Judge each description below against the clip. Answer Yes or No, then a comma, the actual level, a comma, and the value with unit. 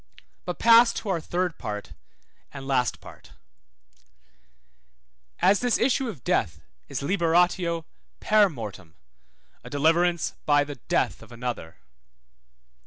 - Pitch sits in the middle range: Yes, medium, 165 Hz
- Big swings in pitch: Yes, wide, 5.9 semitones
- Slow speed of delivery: Yes, slow, 115 wpm